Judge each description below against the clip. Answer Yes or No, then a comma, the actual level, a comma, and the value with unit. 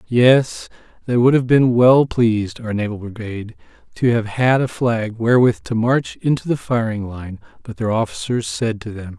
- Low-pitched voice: Yes, low, 115 Hz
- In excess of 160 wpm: Yes, average, 185 wpm